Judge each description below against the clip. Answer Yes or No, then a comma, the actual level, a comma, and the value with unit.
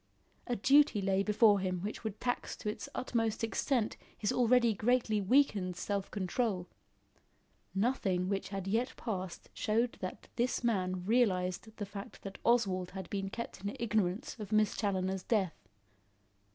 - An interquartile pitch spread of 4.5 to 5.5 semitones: No, average, 3.5 semitones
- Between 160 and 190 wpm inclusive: No, average, 150 wpm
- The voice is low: No, high, 205 Hz